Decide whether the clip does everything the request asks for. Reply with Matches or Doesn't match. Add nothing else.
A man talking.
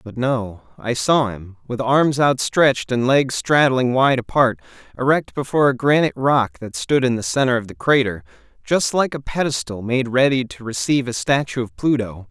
Matches